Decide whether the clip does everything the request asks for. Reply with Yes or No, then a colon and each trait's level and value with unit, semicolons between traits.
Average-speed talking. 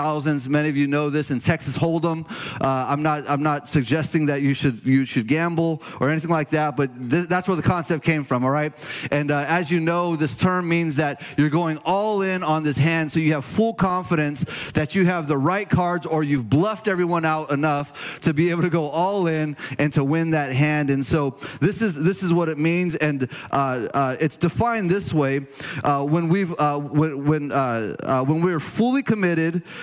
No: fast, 215 wpm